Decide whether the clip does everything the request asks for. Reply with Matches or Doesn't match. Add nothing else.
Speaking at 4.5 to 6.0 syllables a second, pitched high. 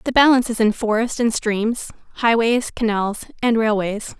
Matches